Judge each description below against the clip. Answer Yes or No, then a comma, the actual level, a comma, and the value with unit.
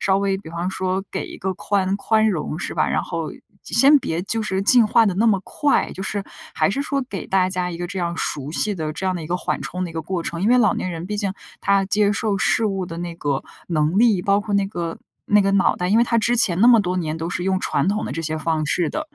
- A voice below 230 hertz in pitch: Yes, high, 190 Hz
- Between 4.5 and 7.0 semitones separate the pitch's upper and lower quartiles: No, average, 3.2 semitones